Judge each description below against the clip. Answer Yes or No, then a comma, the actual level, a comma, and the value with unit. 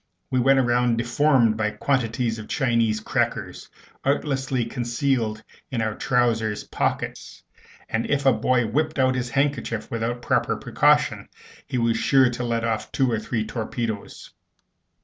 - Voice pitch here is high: No, low, 120 Hz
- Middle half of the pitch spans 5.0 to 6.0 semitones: No, average, 2.7 semitones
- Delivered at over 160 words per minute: No, average, 145 wpm